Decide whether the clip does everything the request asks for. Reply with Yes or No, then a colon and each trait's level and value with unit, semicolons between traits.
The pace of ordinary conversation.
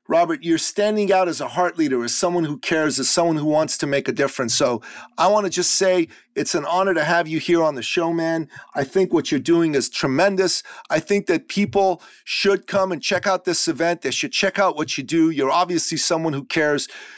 No: fast, 235 wpm